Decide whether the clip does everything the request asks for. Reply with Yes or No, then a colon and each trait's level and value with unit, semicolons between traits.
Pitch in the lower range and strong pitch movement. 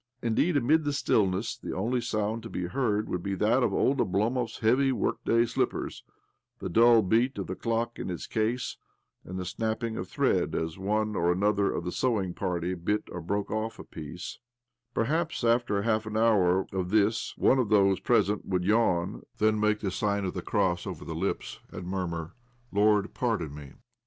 No: low, 105 Hz; average, 3.9 semitones